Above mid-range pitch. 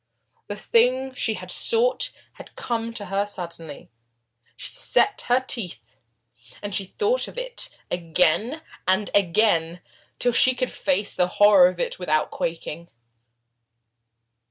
Yes: high, 205 Hz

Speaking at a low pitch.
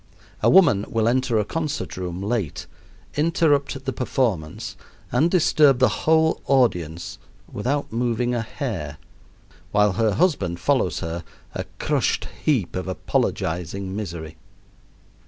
Yes: low, 115 Hz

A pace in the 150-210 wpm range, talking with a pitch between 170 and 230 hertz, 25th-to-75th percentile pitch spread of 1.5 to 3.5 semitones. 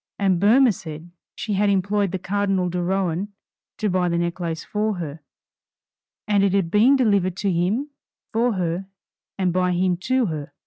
Yes: average, 170 wpm; high, 190 Hz; average, 2.9 semitones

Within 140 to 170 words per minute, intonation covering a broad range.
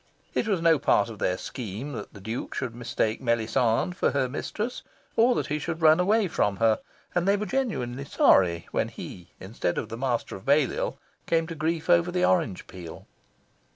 No: average, 190 wpm; wide, 7.5 semitones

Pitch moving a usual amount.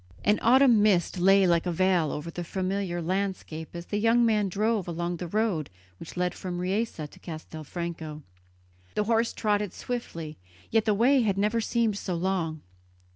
Yes: average, 3.9 semitones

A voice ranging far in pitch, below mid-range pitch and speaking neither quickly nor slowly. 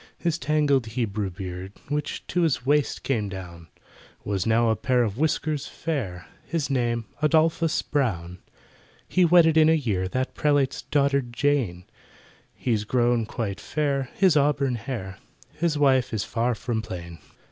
Yes: wide, 5.8 semitones; low, 125 Hz; average, 145 wpm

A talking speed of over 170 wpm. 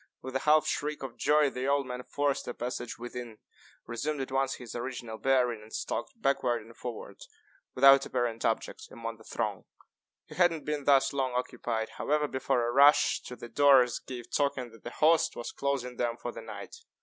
Yes: average, 195 wpm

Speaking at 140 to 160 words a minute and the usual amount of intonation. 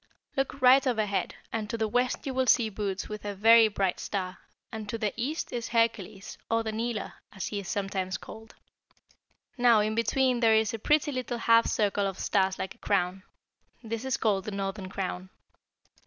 No: average, 190 wpm; average, 3.0 semitones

